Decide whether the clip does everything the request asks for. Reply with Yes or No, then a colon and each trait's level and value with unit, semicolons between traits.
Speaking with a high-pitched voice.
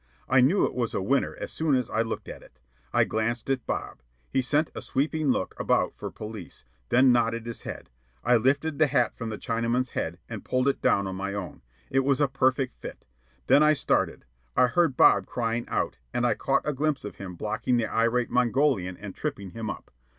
No: low, 125 Hz